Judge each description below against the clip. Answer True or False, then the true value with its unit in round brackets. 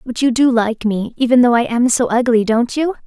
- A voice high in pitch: True (240 Hz)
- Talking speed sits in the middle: False (255 wpm)